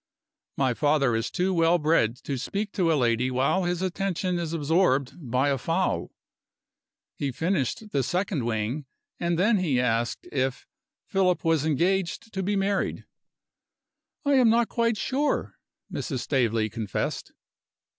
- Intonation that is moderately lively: No, wide, 6.6 semitones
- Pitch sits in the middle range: Yes, medium, 165 Hz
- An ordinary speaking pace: Yes, average, 145 wpm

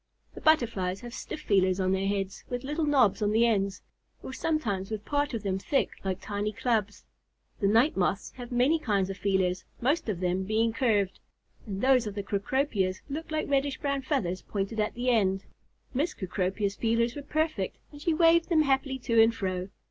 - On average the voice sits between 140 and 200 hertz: No, high, 225 Hz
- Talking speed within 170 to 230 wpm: Yes, average, 195 wpm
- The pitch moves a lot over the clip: Yes, wide, 5.7 semitones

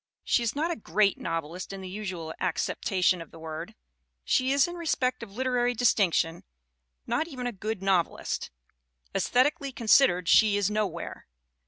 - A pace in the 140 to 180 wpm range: Yes, average, 160 wpm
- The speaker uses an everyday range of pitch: No, wide, 5.9 semitones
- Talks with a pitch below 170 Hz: No, high, 210 Hz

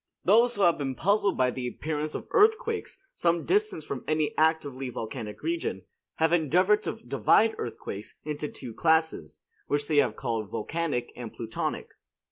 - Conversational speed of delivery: Yes, average, 155 wpm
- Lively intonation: Yes, wide, 7.3 semitones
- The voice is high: No, medium, 155 Hz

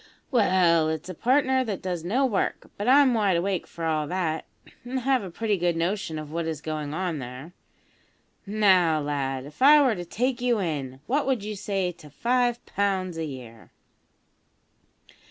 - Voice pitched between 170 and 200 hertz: Yes, medium, 185 Hz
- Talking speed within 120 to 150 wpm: No, average, 175 wpm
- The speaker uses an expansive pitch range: Yes, wide, 6.7 semitones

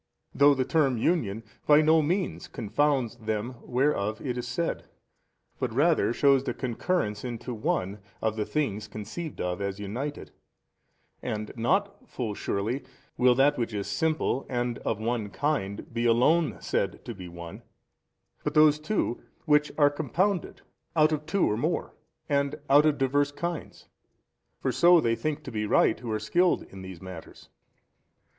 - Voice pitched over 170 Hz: No, low, 125 Hz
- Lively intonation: Yes, wide, 5.8 semitones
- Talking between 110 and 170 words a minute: Yes, average, 160 wpm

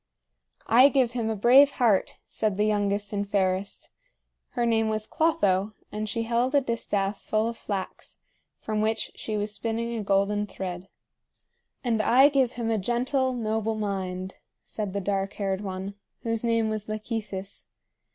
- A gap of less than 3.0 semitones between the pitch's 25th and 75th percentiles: Yes, narrow, 2.6 semitones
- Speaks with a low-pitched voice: No, high, 215 Hz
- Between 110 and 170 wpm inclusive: Yes, average, 160 wpm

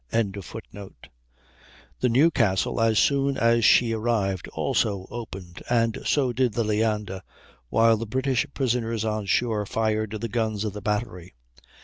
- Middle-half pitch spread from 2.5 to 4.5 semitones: Yes, average, 2.8 semitones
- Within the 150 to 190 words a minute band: No, slow, 135 wpm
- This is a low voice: Yes, low, 110 Hz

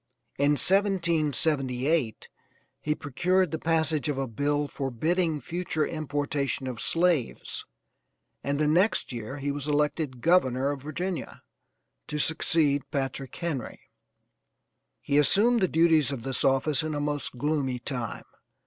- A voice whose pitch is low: No, medium, 145 Hz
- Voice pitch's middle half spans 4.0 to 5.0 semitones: No, average, 3.2 semitones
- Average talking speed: No, slow, 130 wpm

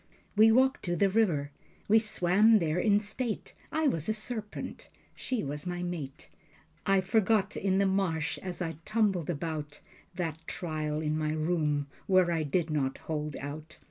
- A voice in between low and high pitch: Yes, medium, 175 Hz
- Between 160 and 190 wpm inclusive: Yes, average, 165 wpm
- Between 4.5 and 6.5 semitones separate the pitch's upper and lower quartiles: Yes, average, 5.1 semitones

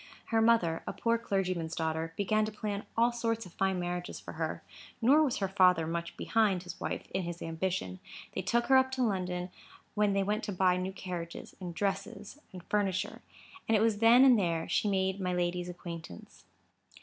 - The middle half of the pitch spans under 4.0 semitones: Yes, average, 3.6 semitones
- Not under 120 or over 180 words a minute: No, average, 195 wpm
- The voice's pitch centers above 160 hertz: Yes, high, 190 Hz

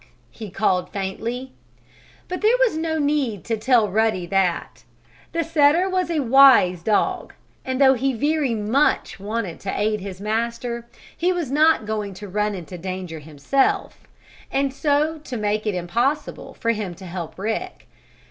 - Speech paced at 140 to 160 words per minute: Yes, average, 155 wpm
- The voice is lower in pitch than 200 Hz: No, high, 230 Hz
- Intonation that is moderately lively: No, wide, 6.5 semitones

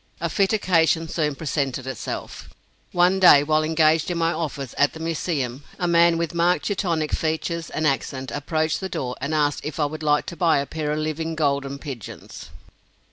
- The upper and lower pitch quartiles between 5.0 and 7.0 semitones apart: No, narrow, 2.6 semitones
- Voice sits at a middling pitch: Yes, medium, 155 Hz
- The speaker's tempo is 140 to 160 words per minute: No, average, 190 wpm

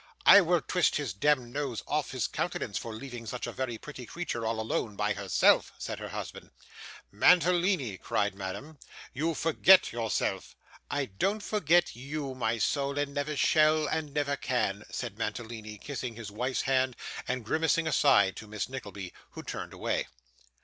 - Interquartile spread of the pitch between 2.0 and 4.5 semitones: No, average, 5.3 semitones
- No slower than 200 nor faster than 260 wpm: No, average, 165 wpm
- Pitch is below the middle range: Yes, low, 130 Hz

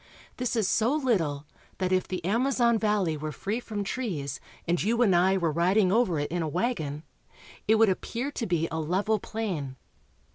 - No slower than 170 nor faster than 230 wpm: Yes, average, 185 wpm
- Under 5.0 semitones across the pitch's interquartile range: No, wide, 5.4 semitones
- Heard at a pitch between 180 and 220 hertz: Yes, high, 190 Hz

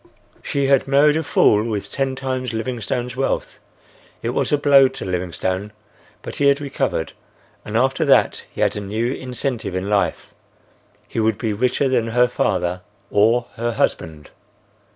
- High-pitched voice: No, low, 120 Hz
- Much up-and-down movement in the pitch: No, average, 4.4 semitones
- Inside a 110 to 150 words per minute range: No, average, 160 wpm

